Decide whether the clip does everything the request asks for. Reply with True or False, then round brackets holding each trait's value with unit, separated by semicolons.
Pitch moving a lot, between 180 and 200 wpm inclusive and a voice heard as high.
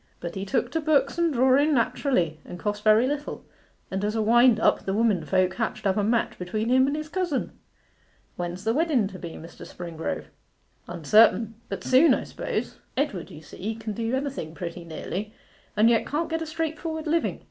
True (7.1 semitones; 190 wpm; 225 Hz)